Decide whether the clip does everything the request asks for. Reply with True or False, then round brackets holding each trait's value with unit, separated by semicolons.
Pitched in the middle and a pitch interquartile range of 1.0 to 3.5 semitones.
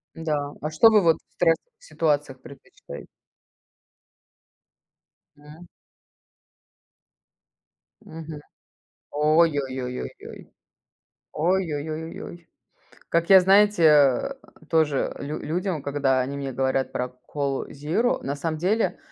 True (150 Hz; 3.1 semitones)